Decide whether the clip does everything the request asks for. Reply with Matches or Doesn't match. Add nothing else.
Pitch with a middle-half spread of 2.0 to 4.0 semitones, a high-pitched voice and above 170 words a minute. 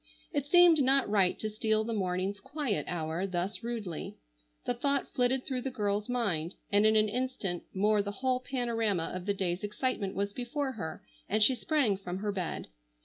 Doesn't match